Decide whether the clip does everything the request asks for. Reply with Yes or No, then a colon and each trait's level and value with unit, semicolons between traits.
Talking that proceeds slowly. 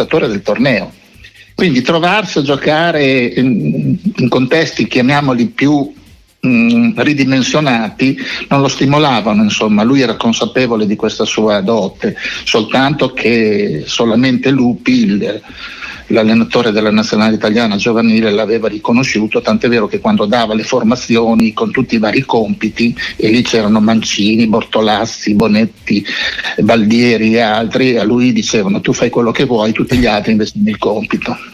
No: average, 135 wpm